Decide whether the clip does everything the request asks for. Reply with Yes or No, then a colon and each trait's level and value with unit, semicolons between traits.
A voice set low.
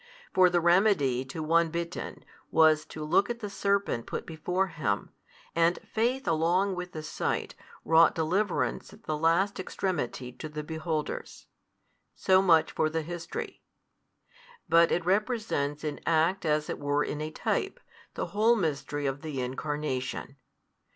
No: medium, 165 Hz